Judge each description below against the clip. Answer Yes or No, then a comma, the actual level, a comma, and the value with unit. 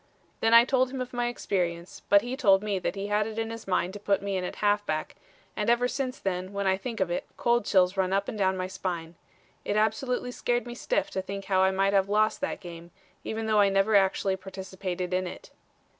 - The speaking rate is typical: No, fast, 235 wpm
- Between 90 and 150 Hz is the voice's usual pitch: No, high, 200 Hz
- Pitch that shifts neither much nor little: Yes, average, 3.0 semitones